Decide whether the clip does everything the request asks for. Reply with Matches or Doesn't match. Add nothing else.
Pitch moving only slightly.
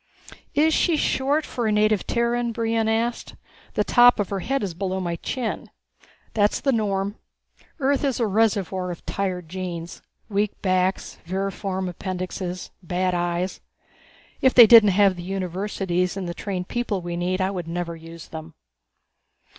Doesn't match